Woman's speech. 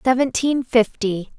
Yes: female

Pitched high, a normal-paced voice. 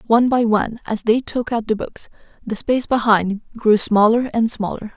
Yes: high, 225 Hz; average, 195 wpm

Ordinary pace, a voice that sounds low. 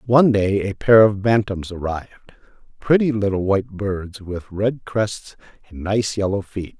Yes: average, 150 wpm; low, 105 Hz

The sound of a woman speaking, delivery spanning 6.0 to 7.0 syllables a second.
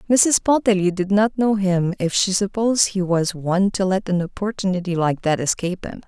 No: female; 5.4 syllables/s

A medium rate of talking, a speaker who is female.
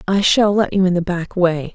No: fast, 275 wpm; female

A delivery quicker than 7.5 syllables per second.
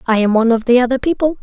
Yes: 8.1 syllables/s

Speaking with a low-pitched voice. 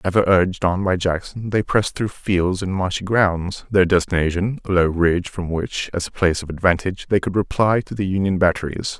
Yes: very low, 95 Hz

